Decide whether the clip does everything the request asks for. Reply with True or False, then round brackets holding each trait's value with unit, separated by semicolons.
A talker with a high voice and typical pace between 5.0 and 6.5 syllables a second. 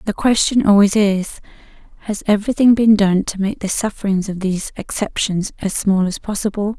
True (205 Hz; 5.3 syllables/s)